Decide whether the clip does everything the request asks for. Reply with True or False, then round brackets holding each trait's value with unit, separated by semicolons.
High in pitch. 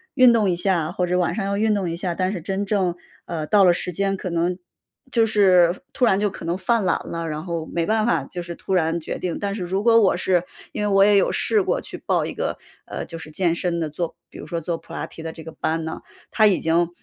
False (180 Hz)